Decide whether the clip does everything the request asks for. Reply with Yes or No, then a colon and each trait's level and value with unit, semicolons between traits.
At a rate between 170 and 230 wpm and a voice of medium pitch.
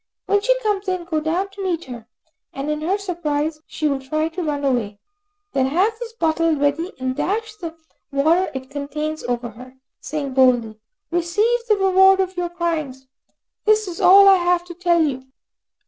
No: average, 180 wpm; very high, 330 Hz